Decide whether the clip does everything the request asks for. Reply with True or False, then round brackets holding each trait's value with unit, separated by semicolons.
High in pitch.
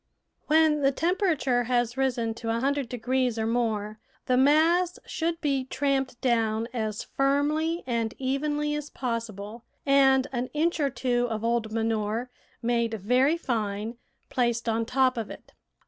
True (250 Hz)